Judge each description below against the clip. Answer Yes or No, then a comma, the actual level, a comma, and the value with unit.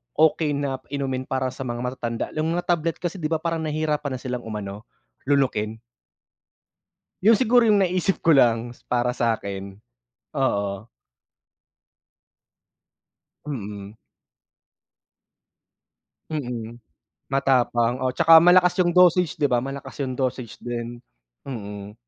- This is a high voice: No, low, 130 Hz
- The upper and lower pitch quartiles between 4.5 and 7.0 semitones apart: Yes, average, 5.2 semitones